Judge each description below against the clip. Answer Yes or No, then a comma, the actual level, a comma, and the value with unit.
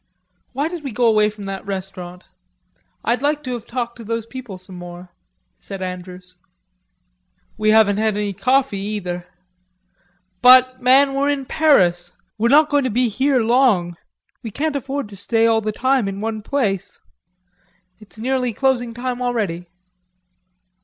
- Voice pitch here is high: Yes, high, 225 Hz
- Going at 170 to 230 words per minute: No, average, 155 wpm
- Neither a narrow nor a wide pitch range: Yes, average, 4.7 semitones